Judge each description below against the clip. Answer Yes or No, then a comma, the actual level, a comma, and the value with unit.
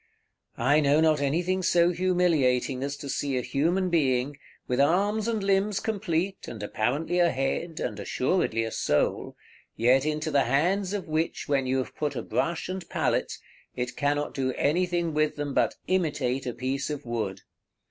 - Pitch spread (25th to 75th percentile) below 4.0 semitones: No, average, 5.1 semitones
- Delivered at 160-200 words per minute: Yes, average, 170 wpm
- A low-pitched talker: No, medium, 150 Hz